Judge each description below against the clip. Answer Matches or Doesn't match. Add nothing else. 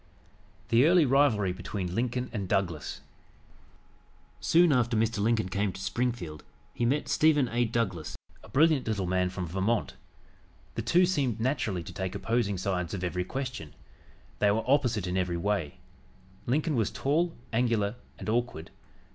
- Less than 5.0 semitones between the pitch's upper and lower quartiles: Doesn't match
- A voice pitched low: Matches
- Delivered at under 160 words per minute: Matches